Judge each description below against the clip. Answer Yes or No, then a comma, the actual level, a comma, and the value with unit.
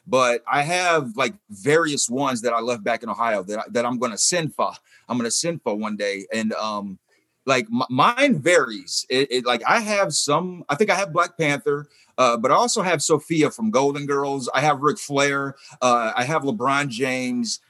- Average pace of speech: No, fast, 215 wpm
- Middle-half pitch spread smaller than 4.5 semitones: No, average, 5.2 semitones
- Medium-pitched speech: Yes, medium, 145 Hz